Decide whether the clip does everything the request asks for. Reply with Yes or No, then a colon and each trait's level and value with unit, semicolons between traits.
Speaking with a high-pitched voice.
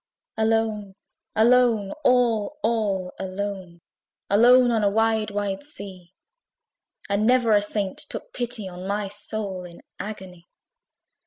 Yes: high, 210 Hz